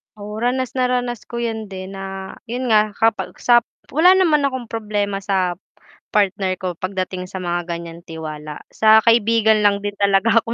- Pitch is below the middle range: No, high, 210 Hz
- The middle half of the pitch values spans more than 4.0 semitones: No, average, 3.7 semitones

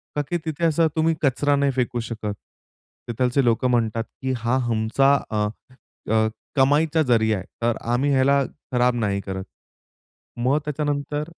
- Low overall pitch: Yes, low, 130 Hz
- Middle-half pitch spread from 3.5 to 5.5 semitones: Yes, average, 3.8 semitones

